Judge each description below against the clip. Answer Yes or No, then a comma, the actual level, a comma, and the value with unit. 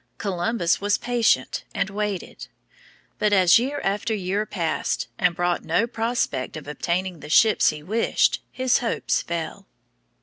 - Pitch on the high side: Yes, high, 195 Hz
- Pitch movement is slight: No, average, 4.5 semitones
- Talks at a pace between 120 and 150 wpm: Yes, average, 140 wpm